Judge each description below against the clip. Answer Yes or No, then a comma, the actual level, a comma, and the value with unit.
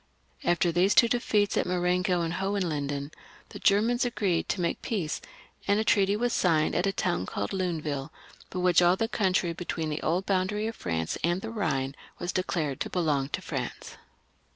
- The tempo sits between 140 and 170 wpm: No, average, 180 wpm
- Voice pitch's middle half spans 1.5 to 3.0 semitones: No, average, 3.9 semitones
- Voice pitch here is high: No, medium, 180 Hz